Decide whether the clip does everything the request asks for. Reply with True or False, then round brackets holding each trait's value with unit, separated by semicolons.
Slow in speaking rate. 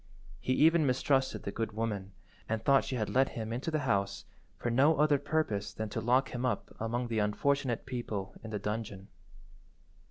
False (185 wpm)